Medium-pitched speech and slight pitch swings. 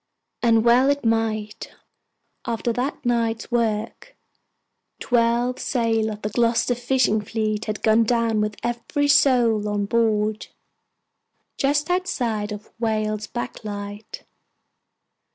No: high, 225 Hz; narrow, 2.1 semitones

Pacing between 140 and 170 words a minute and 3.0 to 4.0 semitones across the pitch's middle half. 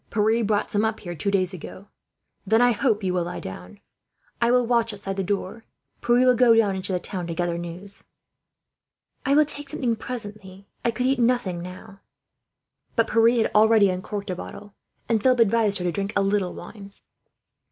No: average, 200 wpm; average, 3.6 semitones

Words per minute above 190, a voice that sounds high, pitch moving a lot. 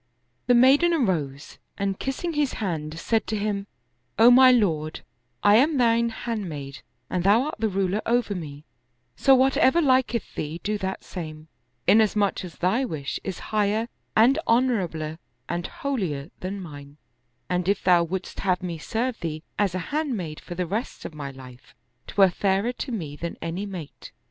No: average, 175 wpm; high, 195 Hz; wide, 6.1 semitones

